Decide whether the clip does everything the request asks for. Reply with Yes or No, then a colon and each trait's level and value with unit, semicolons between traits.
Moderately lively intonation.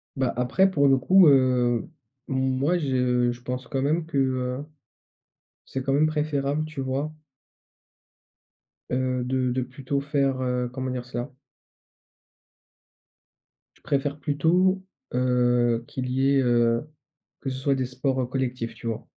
No: narrow, 2.1 semitones